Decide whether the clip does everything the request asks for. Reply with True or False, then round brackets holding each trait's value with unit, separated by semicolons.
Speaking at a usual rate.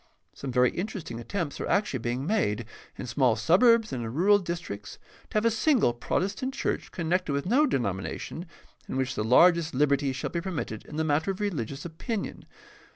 True (180 wpm)